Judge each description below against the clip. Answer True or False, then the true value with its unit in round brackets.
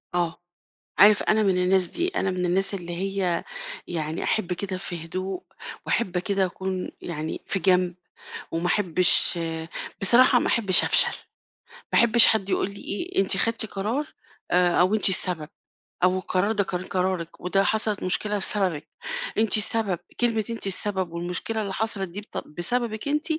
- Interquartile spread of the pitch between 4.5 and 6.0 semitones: False (3.0 semitones)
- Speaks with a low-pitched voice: False (190 Hz)